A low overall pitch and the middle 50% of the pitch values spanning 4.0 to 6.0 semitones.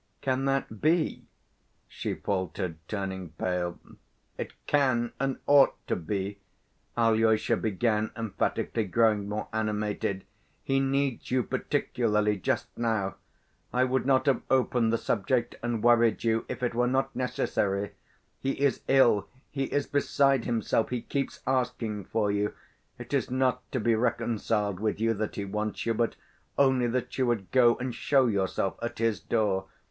No: low, 115 Hz; average, 3.6 semitones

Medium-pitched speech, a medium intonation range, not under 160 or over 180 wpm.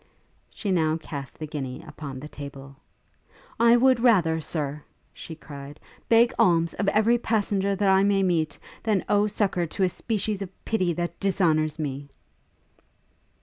No: medium, 175 Hz; average, 5.0 semitones; average, 150 wpm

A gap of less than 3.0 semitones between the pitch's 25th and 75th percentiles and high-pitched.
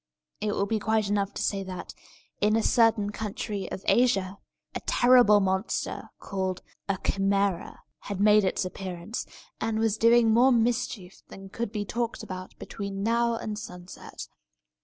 Yes: narrow, 2.6 semitones; high, 205 Hz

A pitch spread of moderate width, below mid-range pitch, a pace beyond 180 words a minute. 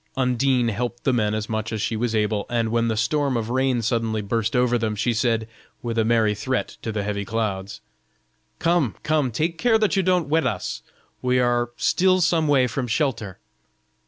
Yes: average, 3.4 semitones; low, 120 Hz; average, 195 wpm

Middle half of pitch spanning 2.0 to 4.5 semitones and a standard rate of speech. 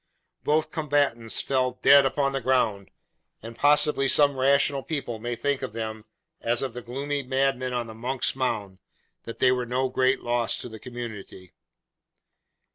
Yes: average, 2.8 semitones; average, 160 wpm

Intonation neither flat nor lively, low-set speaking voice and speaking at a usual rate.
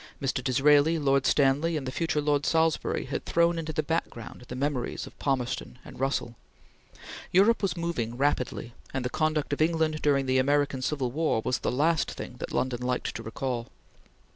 No: average, 3.5 semitones; medium, 145 Hz; average, 180 wpm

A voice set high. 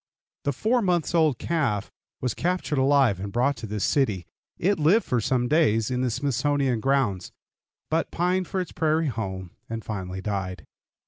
No: low, 130 Hz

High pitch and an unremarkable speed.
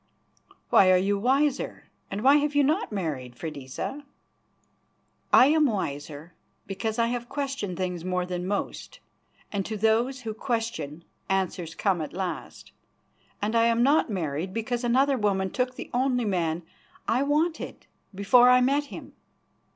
Yes: high, 220 Hz; average, 150 wpm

